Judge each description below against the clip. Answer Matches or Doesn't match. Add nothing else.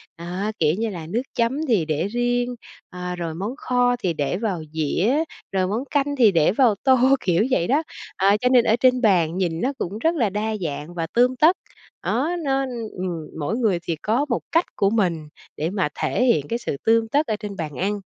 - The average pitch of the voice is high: Matches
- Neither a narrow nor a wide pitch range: Doesn't match